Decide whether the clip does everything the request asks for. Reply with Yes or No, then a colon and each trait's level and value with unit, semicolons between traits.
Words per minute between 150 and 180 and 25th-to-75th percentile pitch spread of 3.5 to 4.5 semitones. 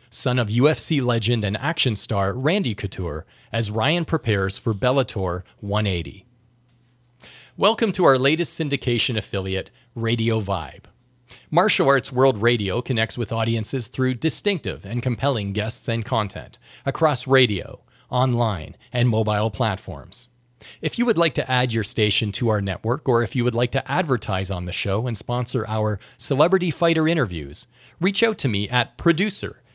Yes: average, 155 wpm; average, 4.0 semitones